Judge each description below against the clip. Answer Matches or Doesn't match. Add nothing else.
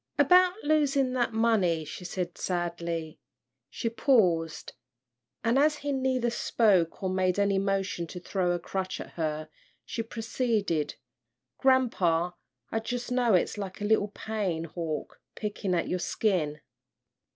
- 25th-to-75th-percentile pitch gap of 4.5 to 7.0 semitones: Matches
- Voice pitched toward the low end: Doesn't match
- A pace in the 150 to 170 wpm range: Doesn't match